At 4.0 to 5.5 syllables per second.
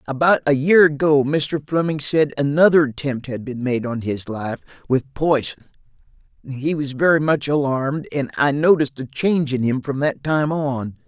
Yes: 4.8 syllables/s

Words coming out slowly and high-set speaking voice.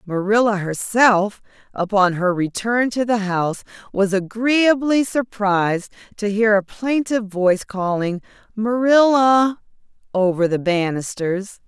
Yes: slow, 110 wpm; high, 210 Hz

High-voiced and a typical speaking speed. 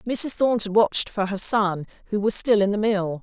No: high, 205 Hz; fast, 225 wpm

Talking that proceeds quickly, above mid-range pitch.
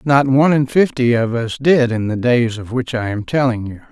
No: fast, 245 wpm; low, 125 Hz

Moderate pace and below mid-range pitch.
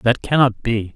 Yes: average, 190 wpm; low, 120 Hz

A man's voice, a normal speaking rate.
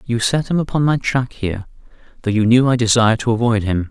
No: male; fast, 230 wpm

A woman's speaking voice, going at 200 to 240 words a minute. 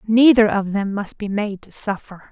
Yes: female; fast, 205 wpm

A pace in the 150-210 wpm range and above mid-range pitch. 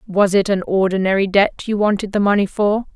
Yes: fast, 205 wpm; high, 200 Hz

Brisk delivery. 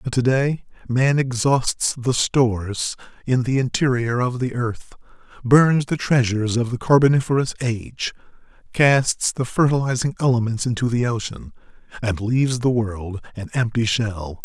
No: average, 140 wpm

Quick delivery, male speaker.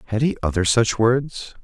No: average, 185 wpm; male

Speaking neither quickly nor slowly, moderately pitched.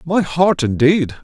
Yes: average, 145 wpm; medium, 155 Hz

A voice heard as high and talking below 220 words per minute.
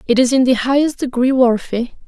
Yes: very high, 255 Hz; average, 200 wpm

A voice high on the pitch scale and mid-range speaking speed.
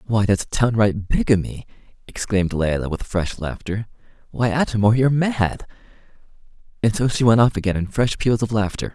No: low, 110 Hz; average, 170 wpm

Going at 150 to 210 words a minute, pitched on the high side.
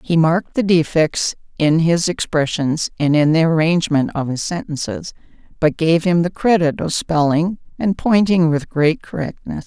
No: average, 160 wpm; medium, 160 Hz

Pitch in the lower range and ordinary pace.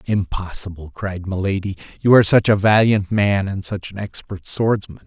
Yes: low, 100 Hz; average, 165 wpm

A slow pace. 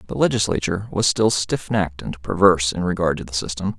No: fast, 205 wpm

